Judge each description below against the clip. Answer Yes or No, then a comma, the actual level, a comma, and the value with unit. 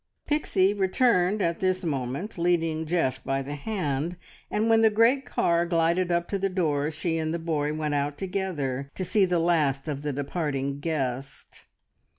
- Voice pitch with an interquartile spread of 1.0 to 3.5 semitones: No, average, 4.4 semitones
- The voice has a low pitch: No, medium, 165 Hz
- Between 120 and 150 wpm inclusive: No, average, 170 wpm